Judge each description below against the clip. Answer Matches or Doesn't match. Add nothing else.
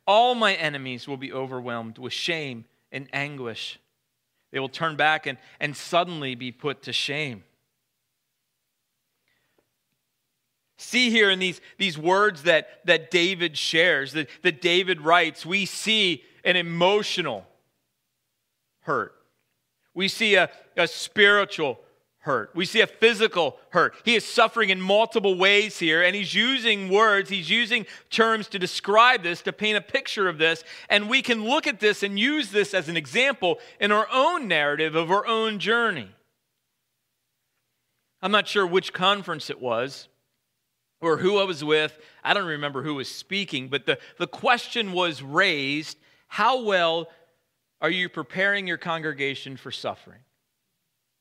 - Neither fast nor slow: Matches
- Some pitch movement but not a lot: Doesn't match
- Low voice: Doesn't match